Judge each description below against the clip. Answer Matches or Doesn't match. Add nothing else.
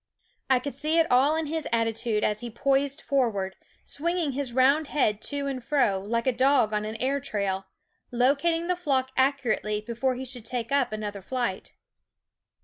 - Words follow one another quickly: Doesn't match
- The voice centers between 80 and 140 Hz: Doesn't match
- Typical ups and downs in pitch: Matches